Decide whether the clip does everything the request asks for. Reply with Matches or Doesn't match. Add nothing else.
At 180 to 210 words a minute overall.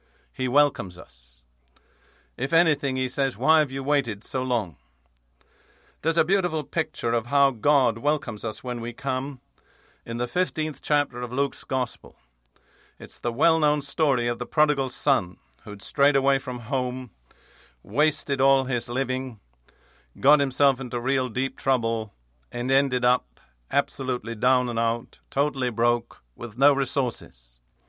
Doesn't match